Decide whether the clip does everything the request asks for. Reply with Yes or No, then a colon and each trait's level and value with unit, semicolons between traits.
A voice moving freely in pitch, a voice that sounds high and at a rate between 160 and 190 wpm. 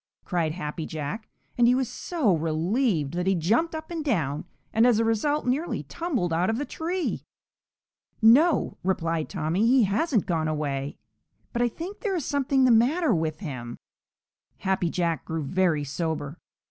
Yes: wide, 8.6 semitones; high, 195 Hz; average, 165 wpm